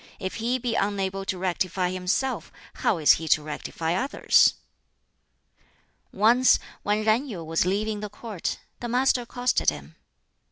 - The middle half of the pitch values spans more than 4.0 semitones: Yes, average, 4.7 semitones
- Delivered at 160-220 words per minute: No, average, 145 wpm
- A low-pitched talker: No, high, 200 Hz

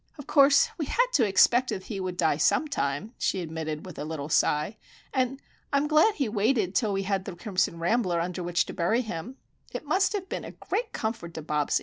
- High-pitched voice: Yes, high, 195 Hz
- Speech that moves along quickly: Yes, fast, 215 wpm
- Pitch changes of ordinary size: No, wide, 7.4 semitones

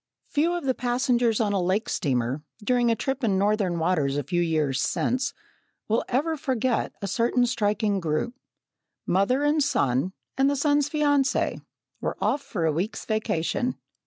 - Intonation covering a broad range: Yes, wide, 7.1 semitones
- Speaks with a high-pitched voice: Yes, high, 225 Hz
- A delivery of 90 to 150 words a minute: No, average, 160 wpm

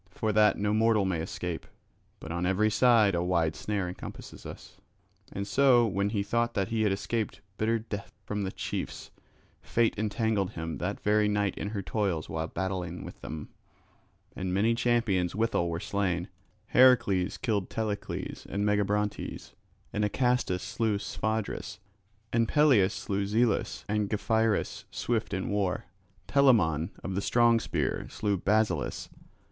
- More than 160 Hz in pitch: No, low, 105 Hz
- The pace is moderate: Yes, average, 150 wpm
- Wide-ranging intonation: No, average, 2.9 semitones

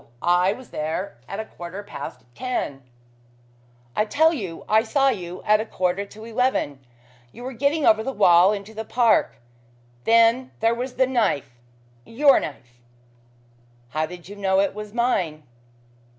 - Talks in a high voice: Yes, high, 210 Hz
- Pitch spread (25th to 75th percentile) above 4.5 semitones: Yes, average, 5.3 semitones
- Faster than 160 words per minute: No, average, 155 wpm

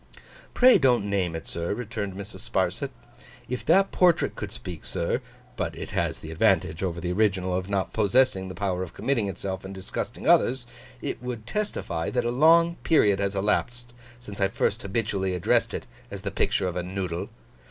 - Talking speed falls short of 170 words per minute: No, average, 175 wpm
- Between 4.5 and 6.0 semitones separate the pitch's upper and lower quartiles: Yes, average, 4.8 semitones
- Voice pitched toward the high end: No, low, 100 Hz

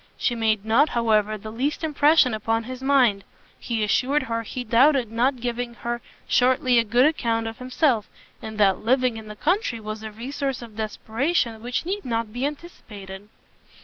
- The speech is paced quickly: No, average, 175 wpm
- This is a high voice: Yes, high, 235 Hz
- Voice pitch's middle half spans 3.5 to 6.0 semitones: No, average, 3.1 semitones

